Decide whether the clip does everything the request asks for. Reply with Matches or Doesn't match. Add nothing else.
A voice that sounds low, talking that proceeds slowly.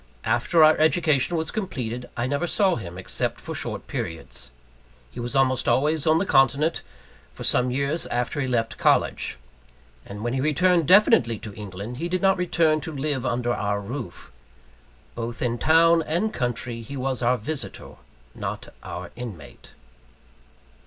Doesn't match